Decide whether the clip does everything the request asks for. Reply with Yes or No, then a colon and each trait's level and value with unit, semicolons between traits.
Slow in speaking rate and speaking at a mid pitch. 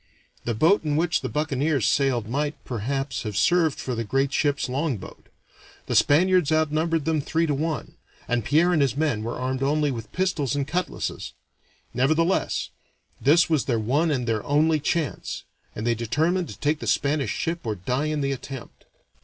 No: average, 180 wpm; medium, 145 Hz